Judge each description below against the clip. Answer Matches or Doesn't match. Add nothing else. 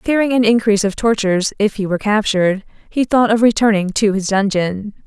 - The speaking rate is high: Doesn't match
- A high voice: Matches